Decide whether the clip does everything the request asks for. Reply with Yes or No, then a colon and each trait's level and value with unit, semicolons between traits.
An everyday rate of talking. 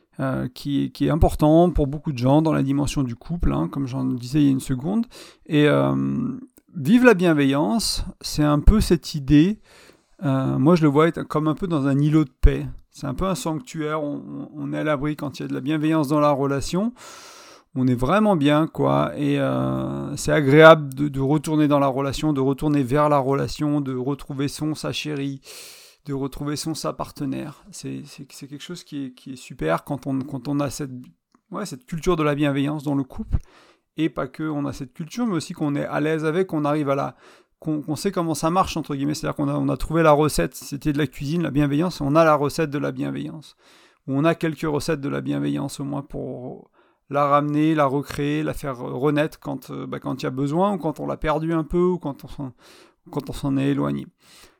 No: fast, 235 wpm